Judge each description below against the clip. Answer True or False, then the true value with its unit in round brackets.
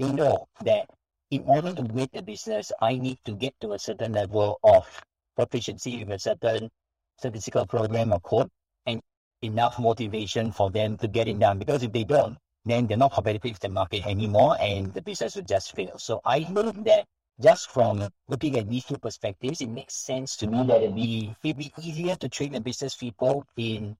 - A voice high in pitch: False (120 Hz)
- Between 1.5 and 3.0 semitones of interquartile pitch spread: False (3.8 semitones)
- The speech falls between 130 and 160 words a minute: False (200 wpm)